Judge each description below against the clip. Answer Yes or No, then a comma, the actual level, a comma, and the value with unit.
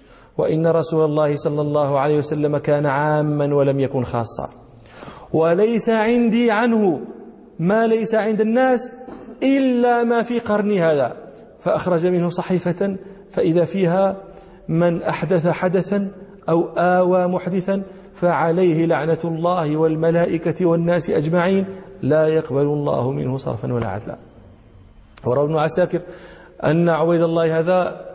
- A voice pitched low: No, medium, 175 Hz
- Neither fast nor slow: No, slow, 115 wpm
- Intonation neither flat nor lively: Yes, average, 3.7 semitones